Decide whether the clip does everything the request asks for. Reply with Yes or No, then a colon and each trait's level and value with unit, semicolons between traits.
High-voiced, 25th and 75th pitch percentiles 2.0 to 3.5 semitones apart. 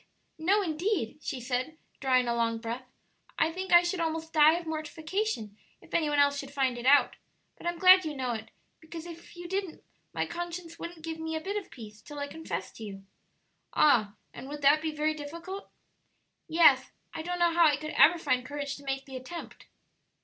No: very high, 310 Hz; average, 4.1 semitones